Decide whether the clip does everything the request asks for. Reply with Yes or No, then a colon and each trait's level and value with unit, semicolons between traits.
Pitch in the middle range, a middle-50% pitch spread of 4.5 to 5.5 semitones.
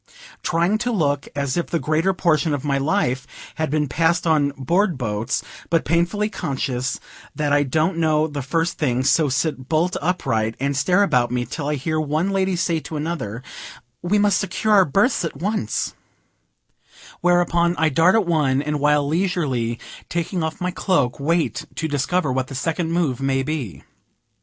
No: medium, 155 Hz; average, 4.1 semitones